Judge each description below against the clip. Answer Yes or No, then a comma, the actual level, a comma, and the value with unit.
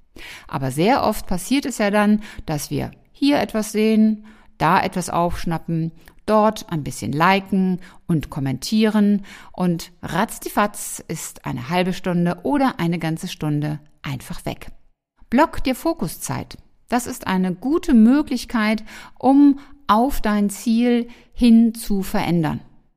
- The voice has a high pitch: Yes, high, 205 Hz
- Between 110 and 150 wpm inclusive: Yes, slow, 125 wpm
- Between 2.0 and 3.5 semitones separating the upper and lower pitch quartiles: No, wide, 5.5 semitones